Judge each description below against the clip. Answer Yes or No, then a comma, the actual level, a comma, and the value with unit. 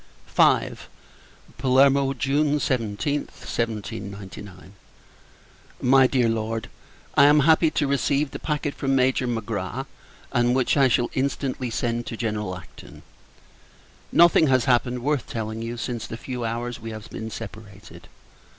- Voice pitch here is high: No, low, 120 Hz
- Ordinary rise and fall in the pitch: Yes, average, 3.4 semitones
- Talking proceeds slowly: Yes, slow, 130 wpm